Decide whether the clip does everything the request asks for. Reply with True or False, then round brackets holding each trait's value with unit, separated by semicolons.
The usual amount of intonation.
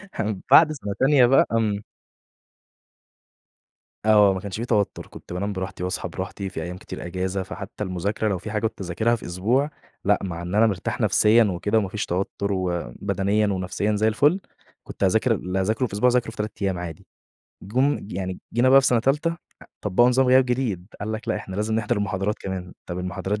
True (3.5 semitones)